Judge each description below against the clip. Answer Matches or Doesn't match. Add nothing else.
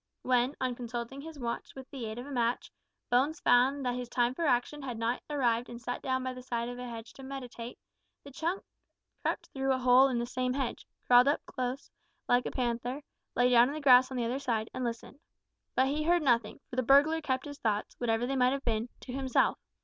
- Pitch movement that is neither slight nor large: Doesn't match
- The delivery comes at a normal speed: Doesn't match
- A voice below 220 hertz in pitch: Doesn't match